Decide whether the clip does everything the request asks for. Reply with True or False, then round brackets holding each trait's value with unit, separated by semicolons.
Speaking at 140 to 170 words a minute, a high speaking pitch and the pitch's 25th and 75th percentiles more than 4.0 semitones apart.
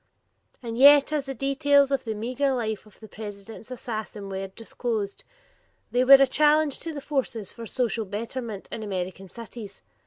True (165 wpm; 235 Hz; 4.4 semitones)